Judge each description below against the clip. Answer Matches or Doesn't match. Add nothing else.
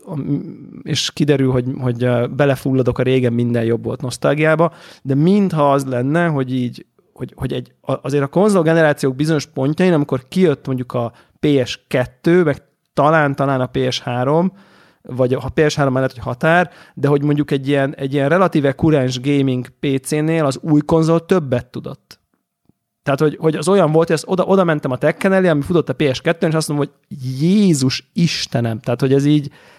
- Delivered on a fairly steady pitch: Doesn't match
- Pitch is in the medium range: Matches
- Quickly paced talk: Matches